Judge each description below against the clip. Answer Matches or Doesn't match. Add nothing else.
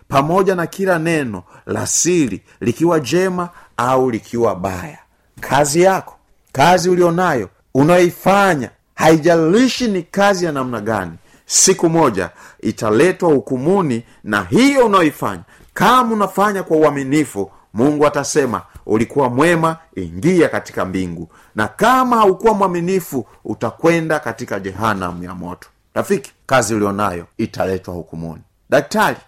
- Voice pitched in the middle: Matches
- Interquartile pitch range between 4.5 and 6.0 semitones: Doesn't match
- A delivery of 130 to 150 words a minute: Doesn't match